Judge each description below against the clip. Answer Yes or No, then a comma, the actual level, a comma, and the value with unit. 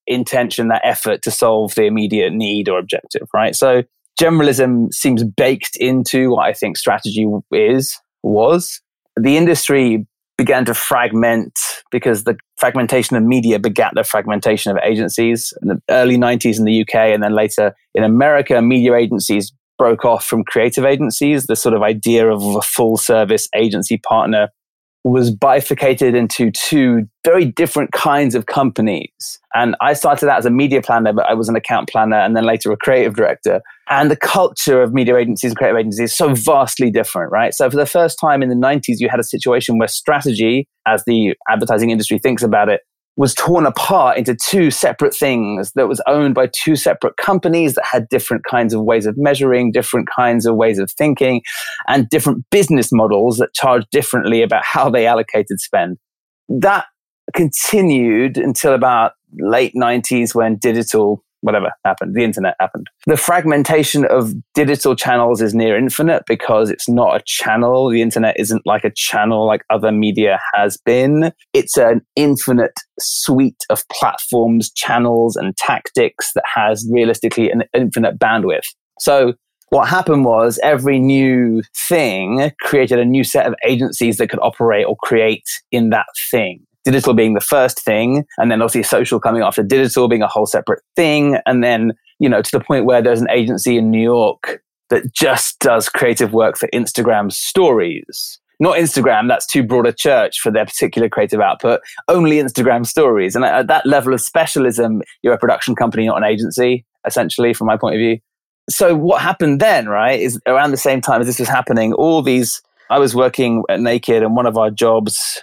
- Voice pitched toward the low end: Yes, low, 120 Hz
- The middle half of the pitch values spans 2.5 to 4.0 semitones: Yes, average, 3.3 semitones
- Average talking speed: Yes, average, 180 wpm